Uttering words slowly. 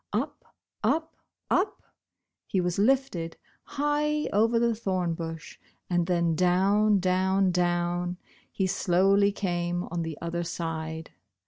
Yes: slow, 120 wpm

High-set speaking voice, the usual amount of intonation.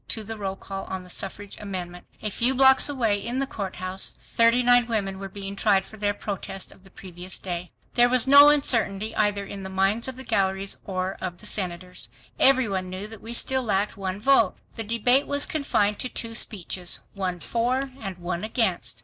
Yes: high, 205 Hz; average, 3.7 semitones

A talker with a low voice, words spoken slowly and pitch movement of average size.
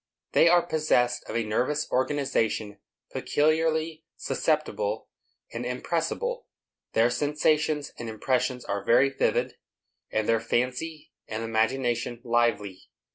Yes: low, 125 Hz; slow, 110 wpm; average, 5.0 semitones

